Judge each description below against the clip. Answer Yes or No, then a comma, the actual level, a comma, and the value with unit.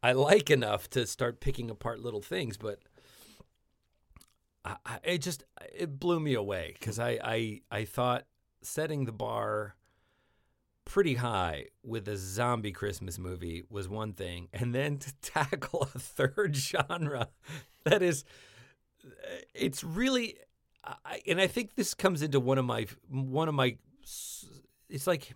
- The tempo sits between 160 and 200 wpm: No, average, 145 wpm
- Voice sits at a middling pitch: No, low, 125 Hz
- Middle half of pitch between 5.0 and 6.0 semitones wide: Yes, wide, 5.4 semitones